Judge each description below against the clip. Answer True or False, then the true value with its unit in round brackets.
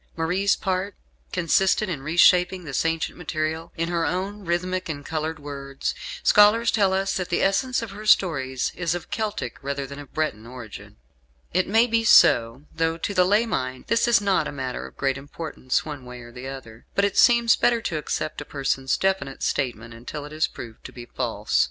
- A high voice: False (165 Hz)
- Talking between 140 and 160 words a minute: False (195 wpm)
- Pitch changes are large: True (6.1 semitones)